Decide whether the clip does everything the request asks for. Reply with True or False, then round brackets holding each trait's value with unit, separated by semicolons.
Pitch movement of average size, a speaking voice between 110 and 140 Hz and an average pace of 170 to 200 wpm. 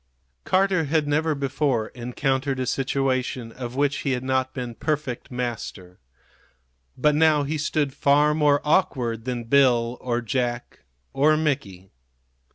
False (3.4 semitones; 135 Hz; 135 wpm)